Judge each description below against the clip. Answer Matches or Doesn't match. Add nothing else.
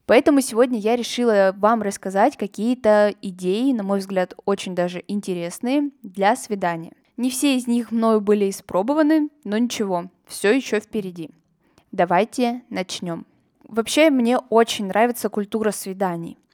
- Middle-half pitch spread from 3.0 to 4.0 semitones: Matches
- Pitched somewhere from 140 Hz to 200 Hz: Doesn't match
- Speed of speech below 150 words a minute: Matches